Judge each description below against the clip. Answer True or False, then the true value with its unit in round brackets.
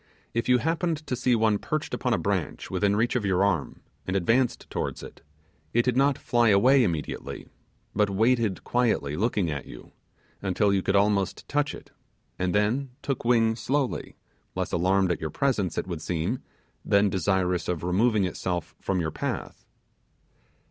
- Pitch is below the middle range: True (105 Hz)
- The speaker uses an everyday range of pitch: True (5.0 semitones)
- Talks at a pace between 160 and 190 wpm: True (170 wpm)